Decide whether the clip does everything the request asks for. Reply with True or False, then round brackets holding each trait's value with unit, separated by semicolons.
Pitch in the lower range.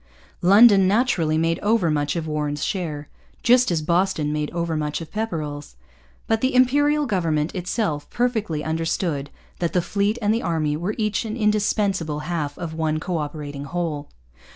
False (170 Hz)